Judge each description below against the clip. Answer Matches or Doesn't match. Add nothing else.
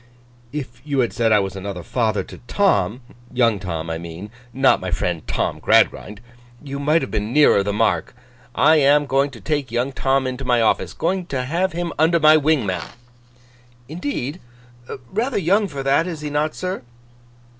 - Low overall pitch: Matches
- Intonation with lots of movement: Matches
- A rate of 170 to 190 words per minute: Matches